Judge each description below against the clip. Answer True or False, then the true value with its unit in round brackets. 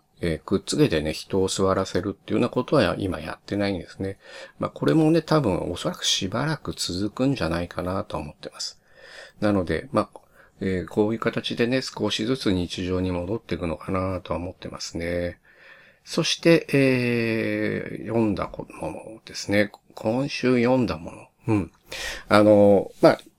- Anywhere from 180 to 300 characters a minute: False (330 characters per minute)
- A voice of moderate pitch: False (105 Hz)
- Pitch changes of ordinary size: True (4.2 semitones)